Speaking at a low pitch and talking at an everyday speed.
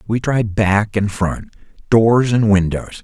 Yes: low, 105 Hz; average, 160 wpm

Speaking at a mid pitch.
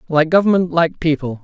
Yes: medium, 160 Hz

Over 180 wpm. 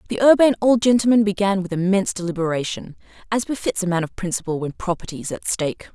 Yes: average, 190 wpm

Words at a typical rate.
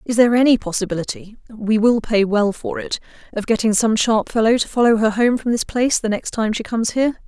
No: fast, 230 wpm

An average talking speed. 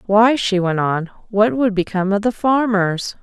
Yes: average, 185 wpm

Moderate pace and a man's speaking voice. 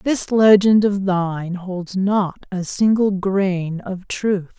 No: average, 145 wpm; female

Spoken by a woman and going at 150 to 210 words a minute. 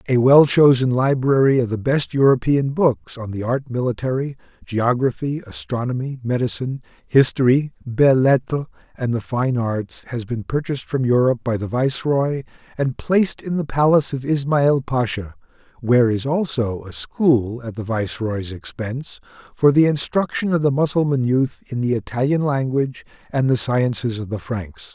No: male; average, 155 wpm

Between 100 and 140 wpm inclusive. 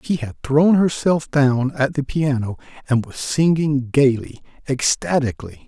Yes: slow, 135 wpm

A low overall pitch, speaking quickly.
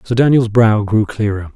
No: low, 110 Hz; average, 195 wpm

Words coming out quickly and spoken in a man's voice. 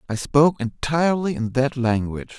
No: average, 150 wpm; male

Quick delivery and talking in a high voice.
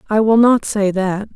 Yes: fast, 220 wpm; high, 210 Hz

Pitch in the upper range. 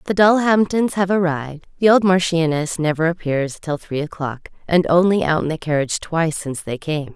No: medium, 165 Hz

